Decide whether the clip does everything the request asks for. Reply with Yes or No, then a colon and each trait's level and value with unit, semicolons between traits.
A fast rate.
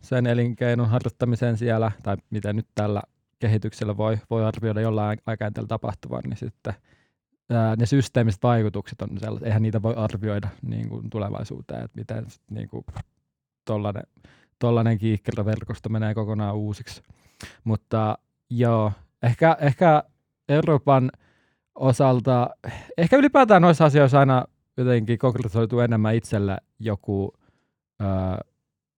No: average, 120 wpm